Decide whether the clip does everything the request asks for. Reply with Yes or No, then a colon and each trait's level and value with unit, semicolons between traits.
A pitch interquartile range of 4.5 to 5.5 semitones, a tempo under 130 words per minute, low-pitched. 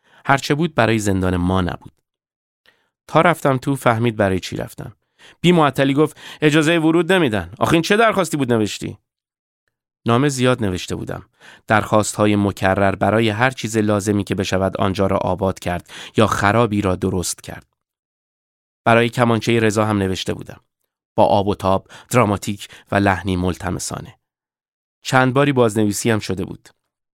No: average, 5.0 semitones; average, 145 wpm; low, 110 Hz